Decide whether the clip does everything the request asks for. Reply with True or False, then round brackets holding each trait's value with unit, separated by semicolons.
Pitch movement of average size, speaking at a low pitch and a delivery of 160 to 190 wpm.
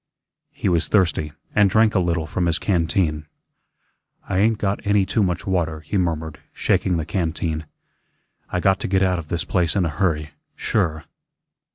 True (3.2 semitones; 85 Hz; 175 wpm)